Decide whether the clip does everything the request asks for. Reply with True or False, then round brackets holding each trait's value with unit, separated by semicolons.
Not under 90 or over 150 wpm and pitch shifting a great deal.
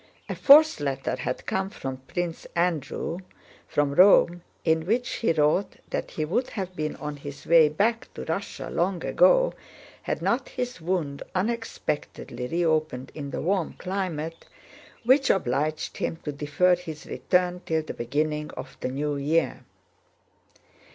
False (145 wpm; 4.1 semitones)